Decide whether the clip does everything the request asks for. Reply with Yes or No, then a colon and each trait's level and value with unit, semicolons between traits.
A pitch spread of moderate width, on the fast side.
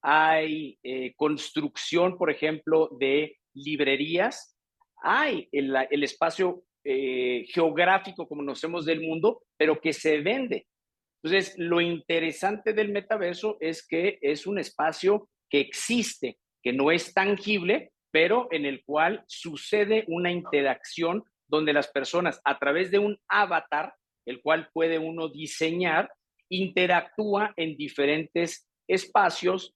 No: average, 4.2 semitones; slow, 125 wpm